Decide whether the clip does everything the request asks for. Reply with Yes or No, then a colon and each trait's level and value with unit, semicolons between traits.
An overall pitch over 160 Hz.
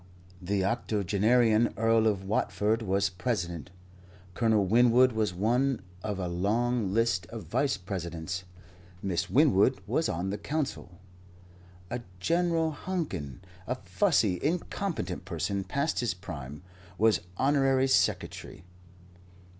No: low, 110 Hz